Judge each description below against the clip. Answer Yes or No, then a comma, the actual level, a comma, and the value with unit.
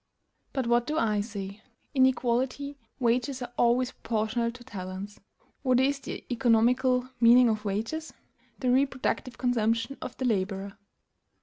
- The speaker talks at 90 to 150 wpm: Yes, slow, 135 wpm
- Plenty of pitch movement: No, average, 2.8 semitones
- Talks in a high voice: Yes, high, 240 Hz